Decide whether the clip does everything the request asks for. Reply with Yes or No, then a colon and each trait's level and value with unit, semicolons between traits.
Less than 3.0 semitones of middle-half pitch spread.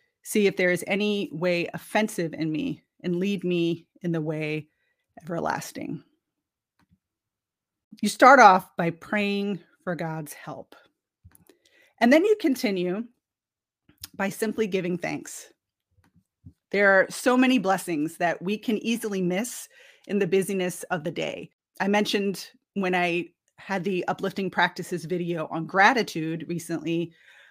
No: average, 3.8 semitones